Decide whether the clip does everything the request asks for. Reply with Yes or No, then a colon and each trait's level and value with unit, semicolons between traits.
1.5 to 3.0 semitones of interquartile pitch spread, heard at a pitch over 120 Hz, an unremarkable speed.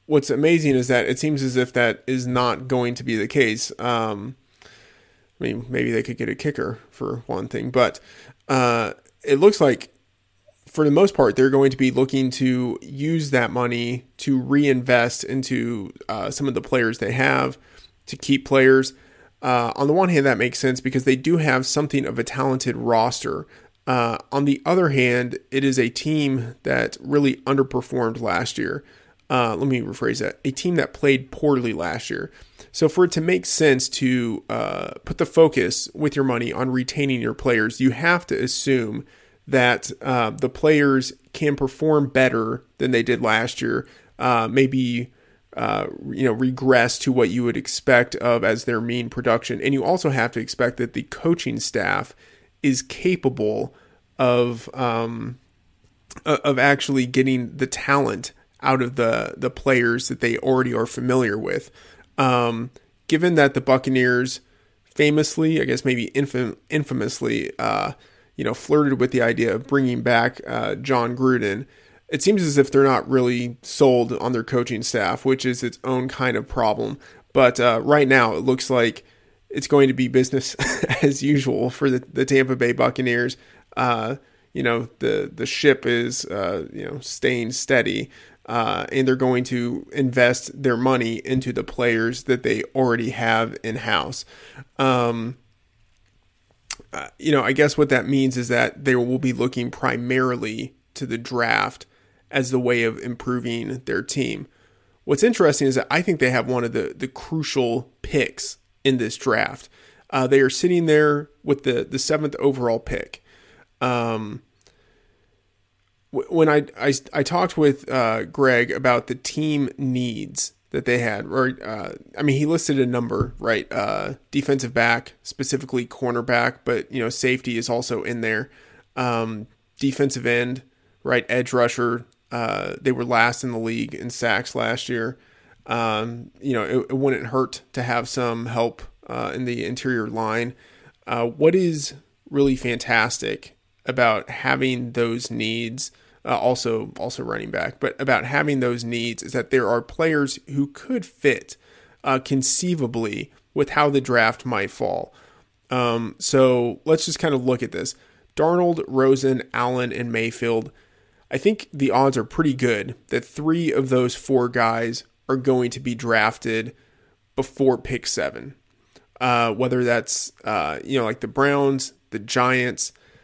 Yes: narrow, 2.4 semitones; low, 130 Hz; average, 165 wpm